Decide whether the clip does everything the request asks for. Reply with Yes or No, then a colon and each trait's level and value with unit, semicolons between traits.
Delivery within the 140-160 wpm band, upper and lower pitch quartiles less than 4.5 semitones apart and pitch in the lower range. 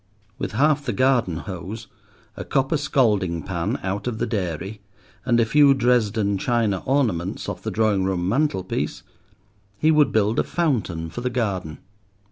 No: average, 155 wpm; average, 5.3 semitones; low, 110 Hz